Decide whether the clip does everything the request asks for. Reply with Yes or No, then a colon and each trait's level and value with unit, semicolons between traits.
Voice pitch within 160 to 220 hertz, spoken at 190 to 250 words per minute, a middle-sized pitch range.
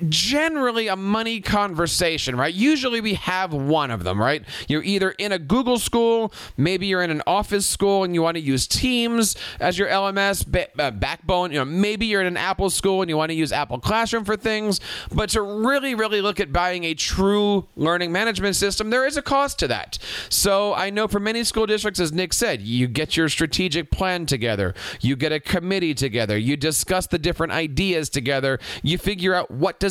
Yes: medium, 185 Hz; fast, 205 wpm; average, 4.8 semitones